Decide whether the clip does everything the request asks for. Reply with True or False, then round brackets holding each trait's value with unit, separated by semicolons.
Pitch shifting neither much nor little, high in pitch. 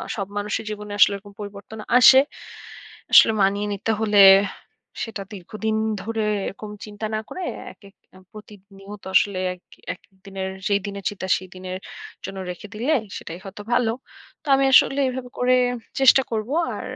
False (2.1 semitones; 205 Hz)